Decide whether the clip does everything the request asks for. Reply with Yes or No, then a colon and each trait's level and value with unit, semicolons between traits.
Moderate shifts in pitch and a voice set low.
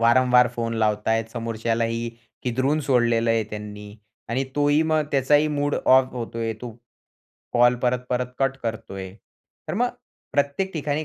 Yes: average, 3.7 semitones; low, 125 Hz